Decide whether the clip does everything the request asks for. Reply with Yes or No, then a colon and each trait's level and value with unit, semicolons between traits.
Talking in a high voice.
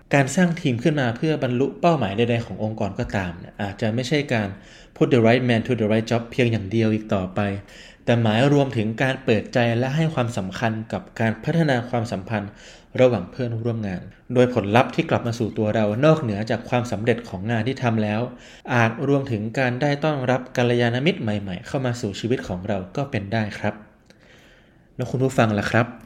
No: low, 115 Hz